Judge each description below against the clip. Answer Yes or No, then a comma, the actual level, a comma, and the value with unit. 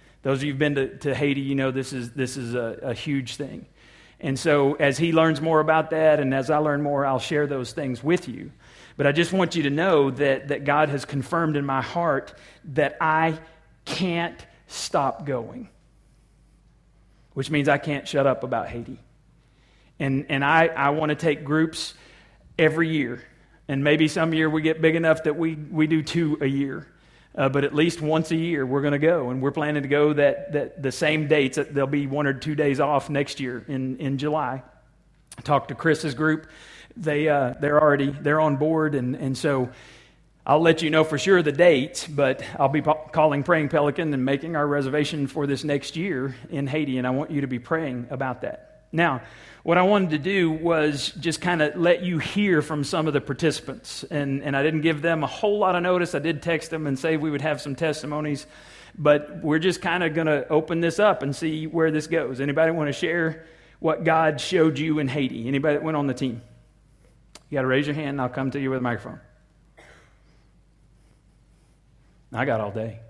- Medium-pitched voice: Yes, medium, 150 Hz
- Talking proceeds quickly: Yes, fast, 215 wpm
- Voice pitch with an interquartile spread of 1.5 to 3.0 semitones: Yes, narrow, 2.5 semitones